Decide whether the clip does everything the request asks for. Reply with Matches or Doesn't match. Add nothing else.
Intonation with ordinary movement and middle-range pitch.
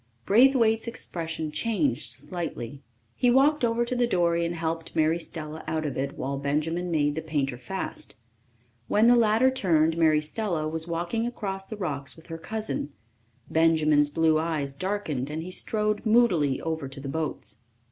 Doesn't match